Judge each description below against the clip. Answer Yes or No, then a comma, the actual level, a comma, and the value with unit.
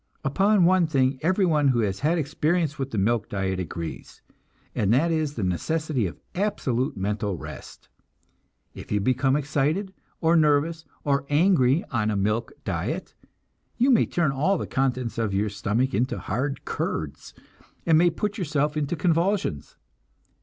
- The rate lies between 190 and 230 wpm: No, average, 155 wpm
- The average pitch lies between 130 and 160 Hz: Yes, medium, 140 Hz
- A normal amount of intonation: No, wide, 6.6 semitones